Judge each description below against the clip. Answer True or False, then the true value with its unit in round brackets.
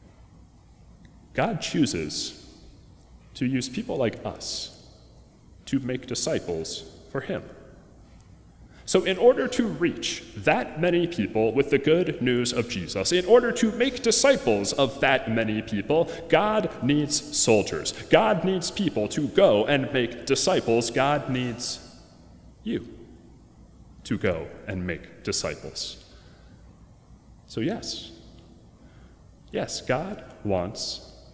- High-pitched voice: False (140 Hz)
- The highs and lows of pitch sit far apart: True (7.4 semitones)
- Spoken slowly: True (115 wpm)